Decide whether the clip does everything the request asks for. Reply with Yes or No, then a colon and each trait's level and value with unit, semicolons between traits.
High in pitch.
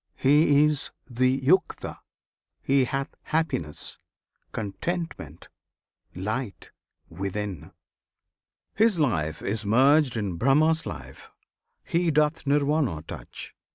No: low, 135 Hz